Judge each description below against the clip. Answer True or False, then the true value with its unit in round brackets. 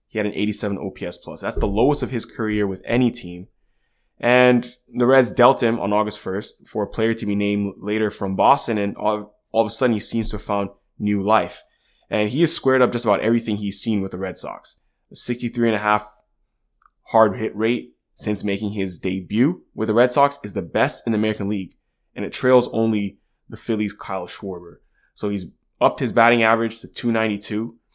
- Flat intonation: True (2.3 semitones)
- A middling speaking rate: False (210 wpm)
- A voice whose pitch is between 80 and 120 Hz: True (110 Hz)